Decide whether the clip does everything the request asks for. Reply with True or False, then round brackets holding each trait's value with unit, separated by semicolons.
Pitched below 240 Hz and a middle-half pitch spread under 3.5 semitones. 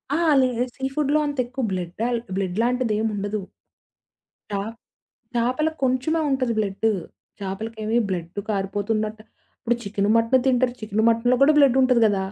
False (230 Hz; 3.8 semitones)